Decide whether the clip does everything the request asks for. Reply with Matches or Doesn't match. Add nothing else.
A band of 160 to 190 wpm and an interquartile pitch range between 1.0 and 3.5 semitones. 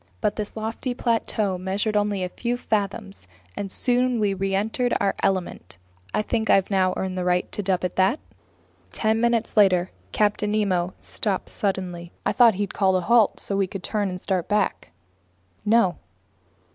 Matches